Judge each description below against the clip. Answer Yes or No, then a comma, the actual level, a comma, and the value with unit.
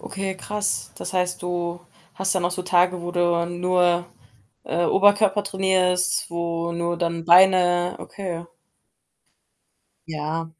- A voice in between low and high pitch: Yes, medium, 175 Hz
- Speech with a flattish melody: Yes, narrow, 1.5 semitones